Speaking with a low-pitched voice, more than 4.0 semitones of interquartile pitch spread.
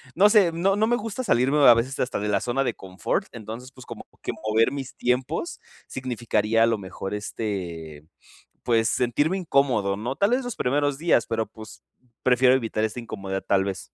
Yes: low, 120 Hz; average, 4.7 semitones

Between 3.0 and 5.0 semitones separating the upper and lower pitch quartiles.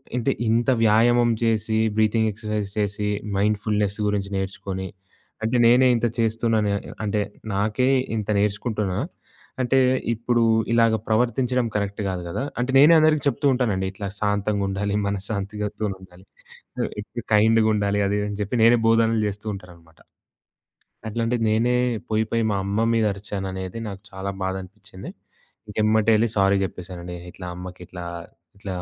No: narrow, 2.6 semitones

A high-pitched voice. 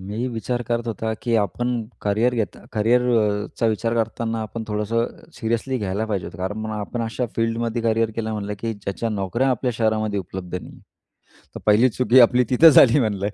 No: low, 115 Hz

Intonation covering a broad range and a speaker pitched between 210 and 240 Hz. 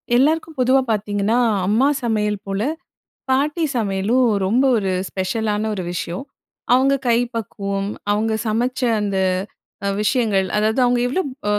No: average, 3.8 semitones; high, 220 Hz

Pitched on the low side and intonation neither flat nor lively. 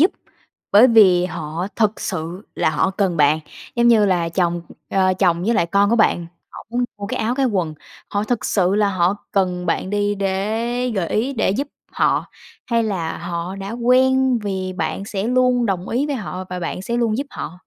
No: high, 200 Hz; average, 4.5 semitones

